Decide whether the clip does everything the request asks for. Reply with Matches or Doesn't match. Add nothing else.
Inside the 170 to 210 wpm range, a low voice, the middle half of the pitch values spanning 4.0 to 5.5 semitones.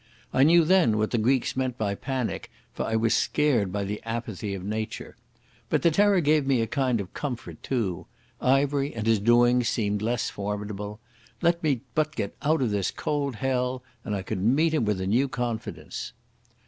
Matches